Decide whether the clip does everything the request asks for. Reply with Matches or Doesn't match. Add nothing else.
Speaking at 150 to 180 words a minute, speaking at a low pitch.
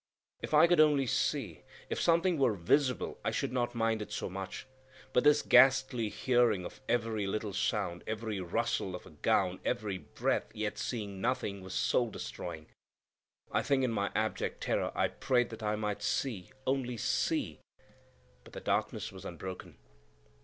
Matches